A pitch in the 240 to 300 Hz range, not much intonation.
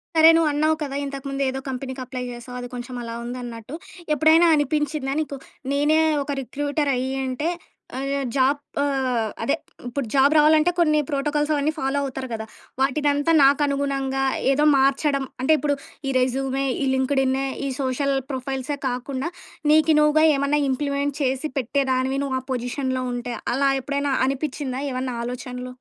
Yes: very high, 275 Hz; narrow, 2.0 semitones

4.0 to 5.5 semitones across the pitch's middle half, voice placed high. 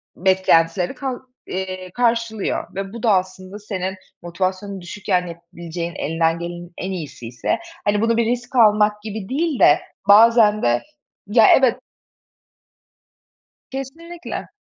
Yes: average, 4.6 semitones; high, 195 Hz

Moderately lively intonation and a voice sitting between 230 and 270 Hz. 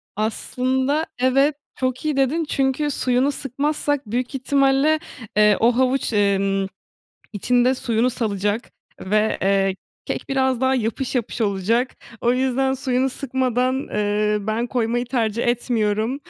Yes: average, 3.6 semitones; very high, 250 Hz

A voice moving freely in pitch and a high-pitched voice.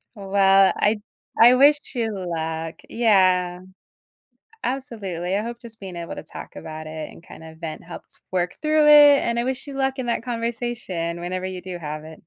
Yes: wide, 5.7 semitones; high, 195 Hz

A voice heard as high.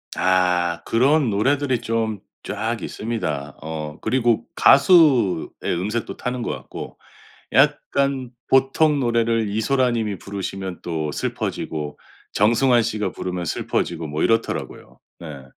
No: low, 110 Hz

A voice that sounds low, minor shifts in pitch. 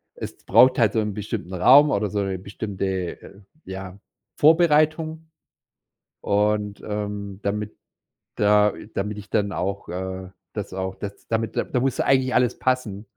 No: low, 105 Hz; average, 4.0 semitones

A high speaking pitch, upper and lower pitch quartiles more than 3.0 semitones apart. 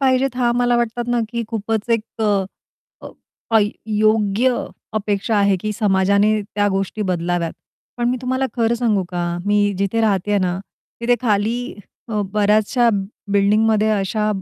No: high, 215 Hz; average, 2.7 semitones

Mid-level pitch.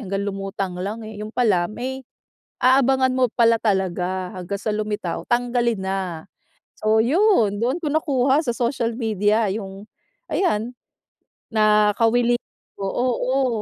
No: high, 225 Hz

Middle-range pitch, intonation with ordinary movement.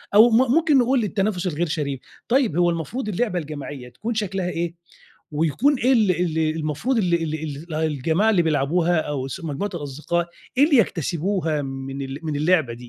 No: medium, 170 Hz; wide, 5.9 semitones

